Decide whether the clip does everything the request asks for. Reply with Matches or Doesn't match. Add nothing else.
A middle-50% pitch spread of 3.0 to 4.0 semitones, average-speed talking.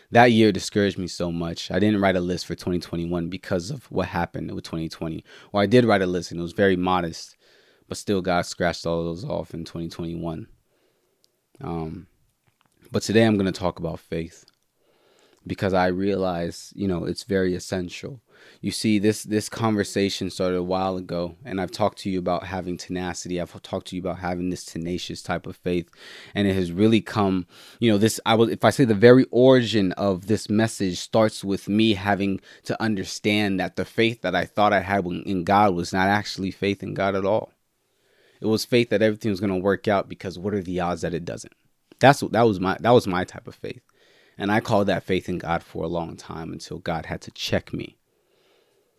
Doesn't match